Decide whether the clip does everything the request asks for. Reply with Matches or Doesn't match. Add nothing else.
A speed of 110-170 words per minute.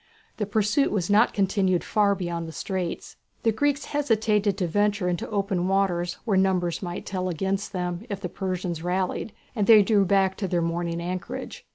Doesn't match